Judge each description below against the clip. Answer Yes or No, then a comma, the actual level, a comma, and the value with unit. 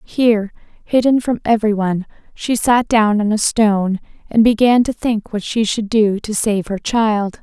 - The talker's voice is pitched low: No, high, 220 Hz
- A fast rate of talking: No, average, 180 wpm